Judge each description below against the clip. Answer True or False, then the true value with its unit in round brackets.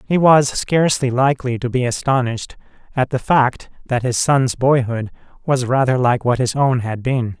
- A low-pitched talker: True (130 Hz)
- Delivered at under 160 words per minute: False (180 wpm)